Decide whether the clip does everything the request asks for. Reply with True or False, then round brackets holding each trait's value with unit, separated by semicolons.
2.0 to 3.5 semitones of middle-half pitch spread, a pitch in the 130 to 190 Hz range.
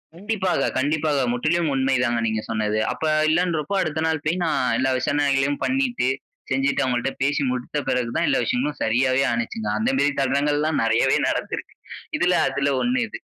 False (3.9 semitones; 140 Hz)